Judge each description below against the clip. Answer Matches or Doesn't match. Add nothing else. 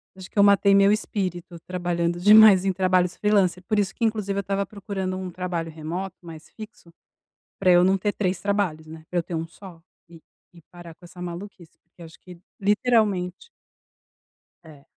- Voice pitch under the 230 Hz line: Matches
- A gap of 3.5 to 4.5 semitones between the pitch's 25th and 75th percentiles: Doesn't match